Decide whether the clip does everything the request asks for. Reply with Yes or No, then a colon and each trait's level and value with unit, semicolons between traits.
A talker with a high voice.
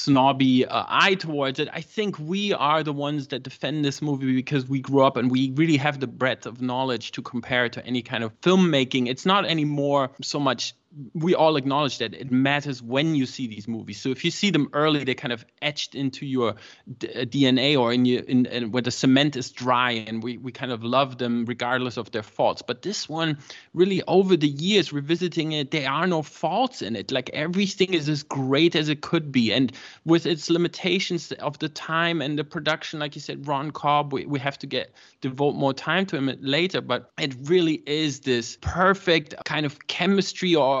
No: medium, 140 Hz